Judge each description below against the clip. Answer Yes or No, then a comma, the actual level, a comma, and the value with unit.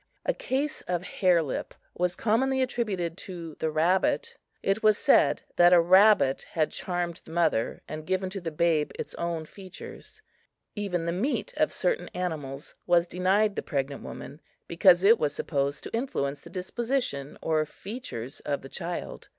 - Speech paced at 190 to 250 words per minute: No, average, 165 wpm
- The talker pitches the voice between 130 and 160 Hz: No, medium, 175 Hz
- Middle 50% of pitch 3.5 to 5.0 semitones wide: Yes, average, 4.6 semitones